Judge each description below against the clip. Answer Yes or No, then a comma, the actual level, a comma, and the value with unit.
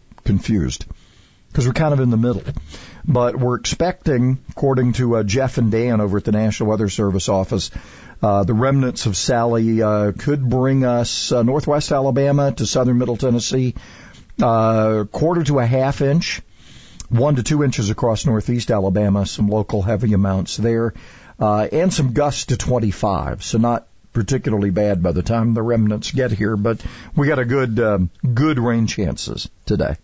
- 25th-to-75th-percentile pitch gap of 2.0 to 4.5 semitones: Yes, average, 3.7 semitones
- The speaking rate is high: No, average, 170 wpm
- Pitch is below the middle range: Yes, low, 115 Hz